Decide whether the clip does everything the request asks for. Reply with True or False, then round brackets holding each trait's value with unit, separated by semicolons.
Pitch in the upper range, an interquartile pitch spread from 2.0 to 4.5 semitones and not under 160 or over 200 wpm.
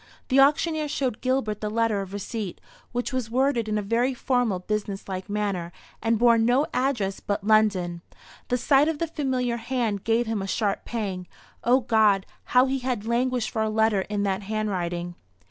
True (225 Hz; 3.7 semitones; 180 wpm)